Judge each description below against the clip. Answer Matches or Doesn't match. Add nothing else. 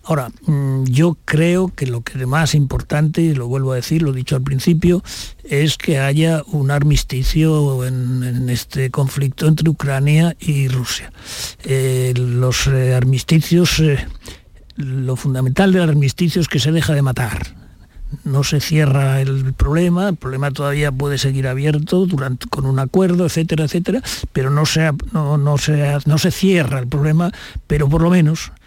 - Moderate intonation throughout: Matches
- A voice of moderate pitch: Matches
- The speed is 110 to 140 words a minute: Doesn't match